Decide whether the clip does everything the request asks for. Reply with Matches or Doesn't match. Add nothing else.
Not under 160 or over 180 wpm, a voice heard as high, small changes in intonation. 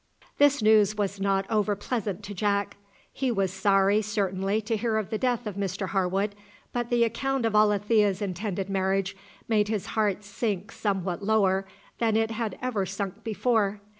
Matches